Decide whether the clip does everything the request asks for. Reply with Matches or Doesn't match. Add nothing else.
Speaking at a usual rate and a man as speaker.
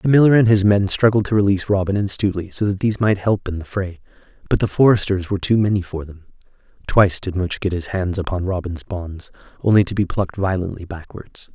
Doesn't match